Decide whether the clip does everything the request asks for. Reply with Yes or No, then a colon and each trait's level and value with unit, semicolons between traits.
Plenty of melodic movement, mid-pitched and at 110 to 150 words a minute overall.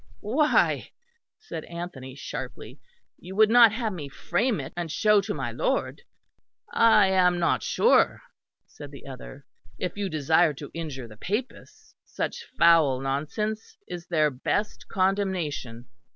Yes: wide, 6.5 semitones; medium, 175 Hz; slow, 135 wpm